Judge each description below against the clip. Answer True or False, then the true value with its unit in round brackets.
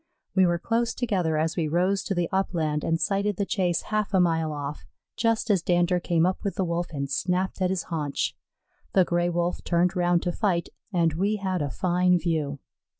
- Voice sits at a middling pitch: True (175 Hz)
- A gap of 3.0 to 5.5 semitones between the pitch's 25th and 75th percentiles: False (2.5 semitones)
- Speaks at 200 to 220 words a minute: True (205 wpm)